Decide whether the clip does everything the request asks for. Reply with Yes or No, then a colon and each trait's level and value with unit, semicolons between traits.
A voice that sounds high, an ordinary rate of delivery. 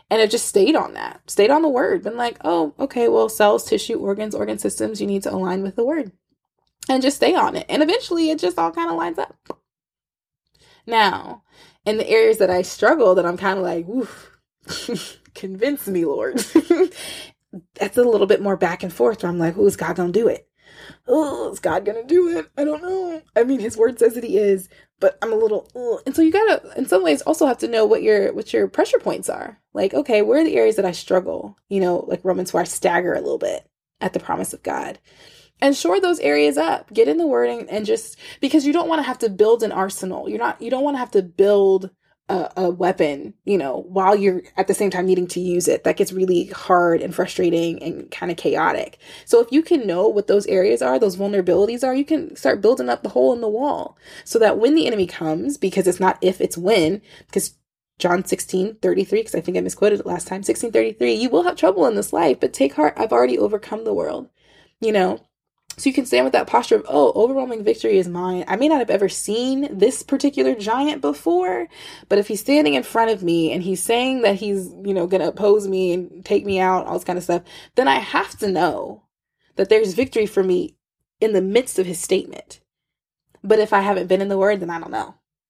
No: high, 205 Hz; fast, 230 wpm